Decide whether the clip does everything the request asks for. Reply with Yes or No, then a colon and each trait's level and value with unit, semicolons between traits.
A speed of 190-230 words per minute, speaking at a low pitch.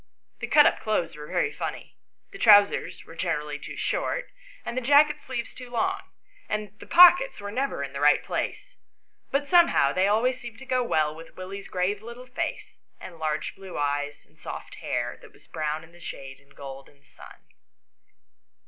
No: average, 195 wpm; high, 200 Hz